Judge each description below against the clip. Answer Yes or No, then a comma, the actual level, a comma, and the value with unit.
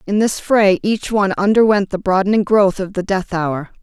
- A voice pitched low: No, high, 195 Hz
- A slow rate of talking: No, fast, 205 wpm